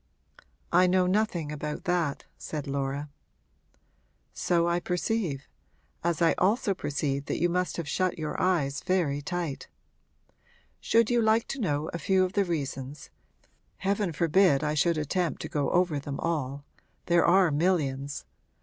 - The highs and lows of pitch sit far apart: No, average, 4.1 semitones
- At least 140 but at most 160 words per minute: Yes, average, 150 wpm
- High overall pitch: No, medium, 170 Hz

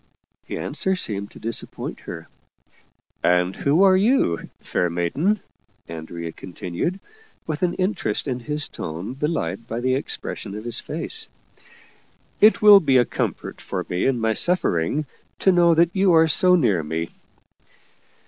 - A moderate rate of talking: Yes, average, 160 wpm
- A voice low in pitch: Yes, low, 130 Hz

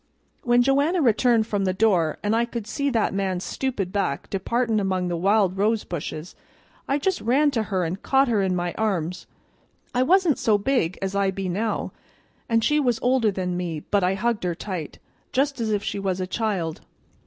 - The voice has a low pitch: No, high, 205 Hz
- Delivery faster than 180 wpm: Yes, average, 200 wpm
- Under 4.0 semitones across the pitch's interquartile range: No, average, 4.6 semitones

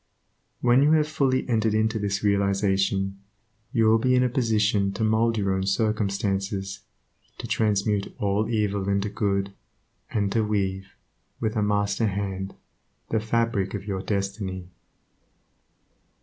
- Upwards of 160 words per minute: No, slow, 135 wpm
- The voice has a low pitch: Yes, low, 105 Hz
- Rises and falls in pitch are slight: Yes, narrow, 2.1 semitones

